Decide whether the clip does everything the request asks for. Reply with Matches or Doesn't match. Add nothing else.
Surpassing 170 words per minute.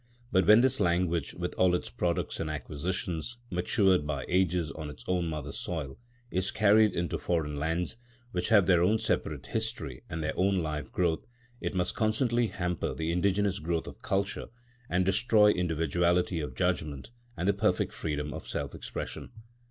Doesn't match